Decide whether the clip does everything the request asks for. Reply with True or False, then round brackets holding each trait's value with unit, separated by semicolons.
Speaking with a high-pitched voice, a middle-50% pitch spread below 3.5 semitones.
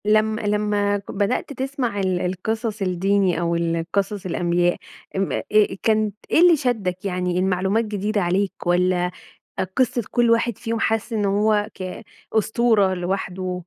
True (200 Hz; 3.1 semitones)